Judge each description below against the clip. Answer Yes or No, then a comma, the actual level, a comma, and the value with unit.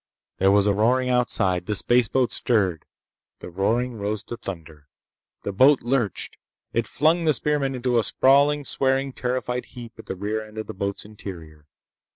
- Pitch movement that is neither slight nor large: Yes, average, 4.5 semitones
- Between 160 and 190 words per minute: Yes, average, 170 wpm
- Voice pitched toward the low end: Yes, low, 115 Hz